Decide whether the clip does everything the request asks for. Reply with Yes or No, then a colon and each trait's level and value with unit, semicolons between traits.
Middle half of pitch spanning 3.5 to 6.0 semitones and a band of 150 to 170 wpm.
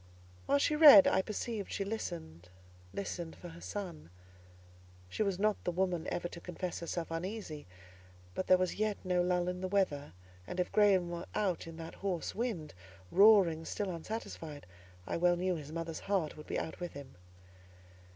Yes: average, 4.0 semitones; average, 165 wpm